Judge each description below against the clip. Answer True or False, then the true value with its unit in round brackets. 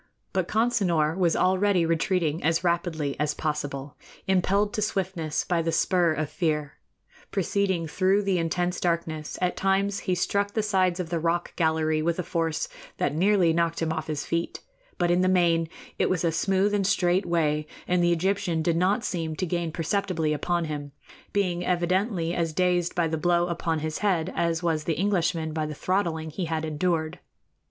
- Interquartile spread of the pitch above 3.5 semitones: False (2.6 semitones)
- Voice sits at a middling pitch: True (170 Hz)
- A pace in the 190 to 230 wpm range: False (180 wpm)